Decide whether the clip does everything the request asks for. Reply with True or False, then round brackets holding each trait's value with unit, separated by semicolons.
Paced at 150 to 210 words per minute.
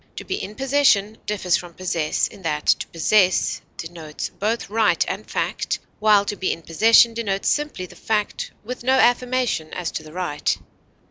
True (175 wpm)